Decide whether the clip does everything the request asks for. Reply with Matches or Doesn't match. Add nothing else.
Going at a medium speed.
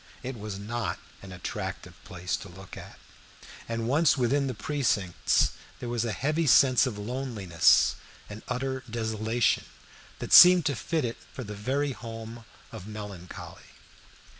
Matches